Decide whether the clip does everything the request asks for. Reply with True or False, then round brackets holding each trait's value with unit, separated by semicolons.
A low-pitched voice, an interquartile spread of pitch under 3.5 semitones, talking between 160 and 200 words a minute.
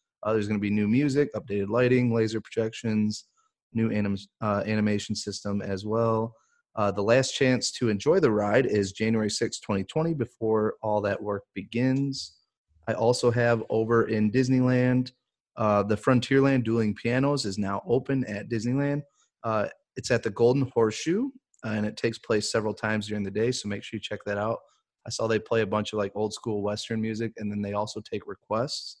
True (110 Hz; 2.9 semitones; 190 wpm)